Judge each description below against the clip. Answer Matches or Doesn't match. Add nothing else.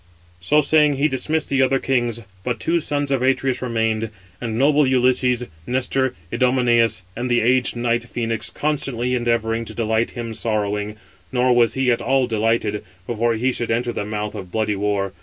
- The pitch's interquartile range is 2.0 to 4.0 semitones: Matches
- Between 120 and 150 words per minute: Doesn't match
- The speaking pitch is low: Matches